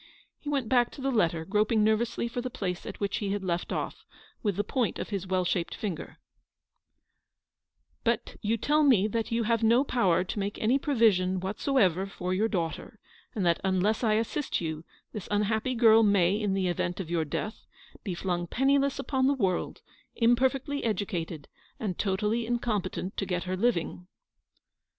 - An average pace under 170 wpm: No, average, 185 wpm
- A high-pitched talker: Yes, high, 210 Hz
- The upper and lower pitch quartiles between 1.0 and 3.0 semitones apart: No, average, 4.3 semitones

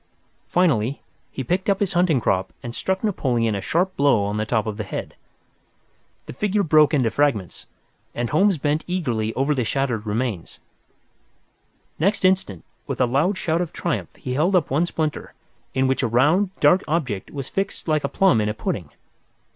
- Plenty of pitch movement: Yes, wide, 7.3 semitones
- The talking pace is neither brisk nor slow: Yes, average, 180 wpm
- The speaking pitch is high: No, medium, 140 Hz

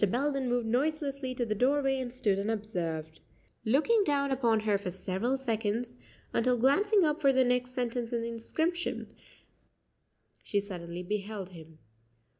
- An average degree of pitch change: Yes, average, 4.7 semitones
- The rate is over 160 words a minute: No, average, 145 wpm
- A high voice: Yes, high, 240 Hz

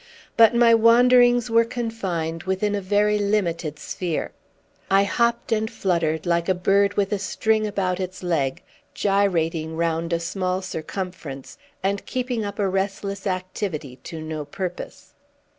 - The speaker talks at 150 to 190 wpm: No, average, 140 wpm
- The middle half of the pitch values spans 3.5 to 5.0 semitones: Yes, average, 3.8 semitones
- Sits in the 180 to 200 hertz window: Yes, high, 190 Hz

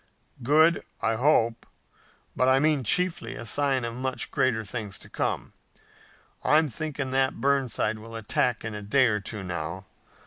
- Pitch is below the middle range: Yes, low, 125 Hz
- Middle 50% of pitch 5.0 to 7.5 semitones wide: No, average, 4.2 semitones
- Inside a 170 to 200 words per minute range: No, average, 160 wpm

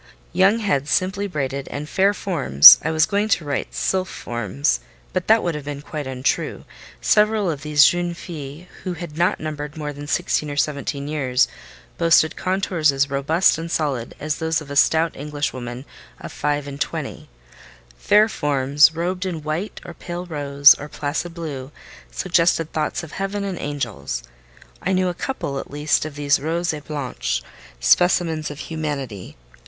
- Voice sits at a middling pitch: Yes, medium, 150 Hz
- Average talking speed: Yes, average, 165 wpm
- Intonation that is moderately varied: Yes, average, 3.7 semitones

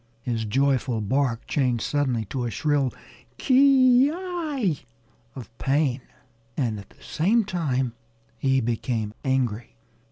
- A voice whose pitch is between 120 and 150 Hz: Yes, low, 135 Hz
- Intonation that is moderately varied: No, wide, 6.9 semitones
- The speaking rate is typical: No, slow, 120 wpm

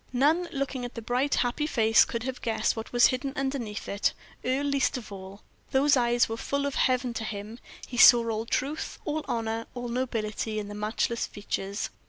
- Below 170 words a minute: No, average, 195 wpm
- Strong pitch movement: No, average, 3.2 semitones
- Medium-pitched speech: No, high, 240 Hz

